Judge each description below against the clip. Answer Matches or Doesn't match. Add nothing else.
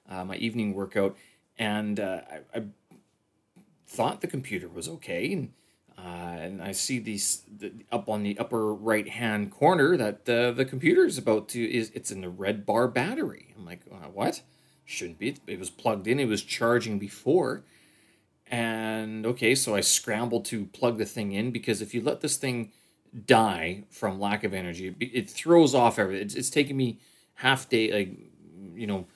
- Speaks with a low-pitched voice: Matches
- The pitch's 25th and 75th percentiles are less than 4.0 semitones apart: Matches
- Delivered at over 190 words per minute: Doesn't match